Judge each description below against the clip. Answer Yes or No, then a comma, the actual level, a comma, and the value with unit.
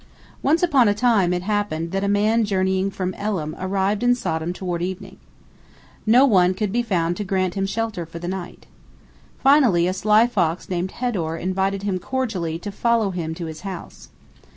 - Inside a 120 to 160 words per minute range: No, average, 180 wpm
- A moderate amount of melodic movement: Yes, average, 3.3 semitones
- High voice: Yes, high, 195 Hz